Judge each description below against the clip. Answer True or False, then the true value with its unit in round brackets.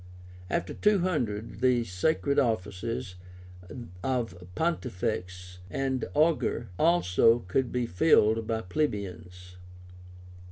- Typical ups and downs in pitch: False (6.7 semitones)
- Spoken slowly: True (85 wpm)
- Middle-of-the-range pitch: False (115 Hz)